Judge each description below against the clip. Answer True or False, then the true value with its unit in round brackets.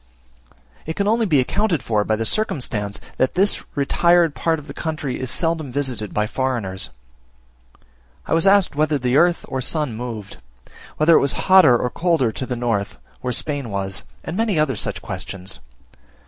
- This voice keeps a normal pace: True (175 wpm)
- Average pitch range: False (6.0 semitones)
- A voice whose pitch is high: False (140 Hz)